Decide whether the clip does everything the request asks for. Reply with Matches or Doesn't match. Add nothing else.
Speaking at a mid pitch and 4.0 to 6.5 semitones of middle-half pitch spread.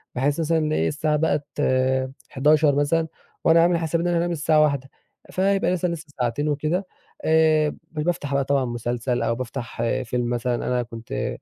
Matches